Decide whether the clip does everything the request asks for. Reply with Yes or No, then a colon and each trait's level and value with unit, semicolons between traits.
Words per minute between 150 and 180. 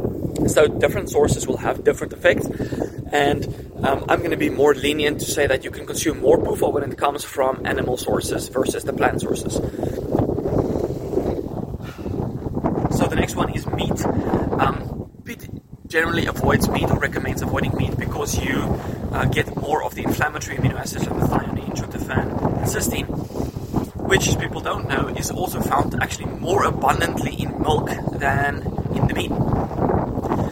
Yes: average, 155 wpm